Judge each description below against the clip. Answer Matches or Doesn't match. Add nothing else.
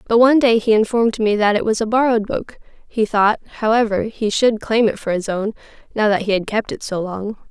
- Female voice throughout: Matches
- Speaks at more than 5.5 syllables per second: Matches